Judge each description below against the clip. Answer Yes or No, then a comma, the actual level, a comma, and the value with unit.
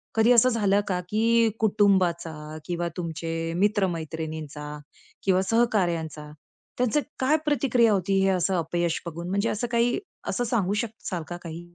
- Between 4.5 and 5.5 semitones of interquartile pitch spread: Yes, average, 5.1 semitones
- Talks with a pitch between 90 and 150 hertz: No, high, 190 Hz